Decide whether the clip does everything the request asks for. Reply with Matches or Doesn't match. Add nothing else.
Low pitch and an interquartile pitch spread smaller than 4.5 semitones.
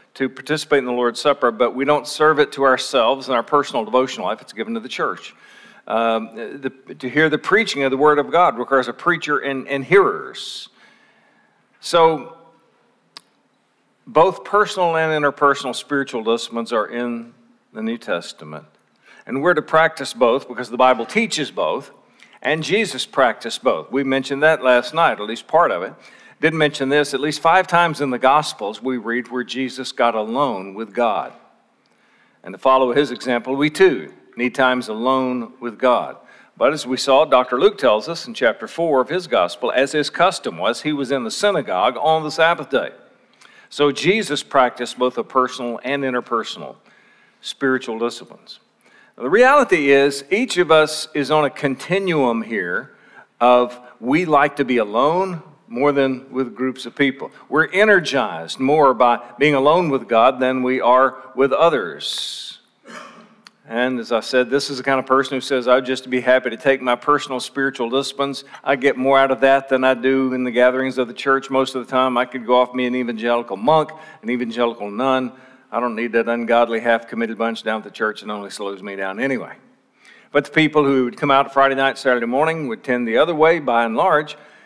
Matches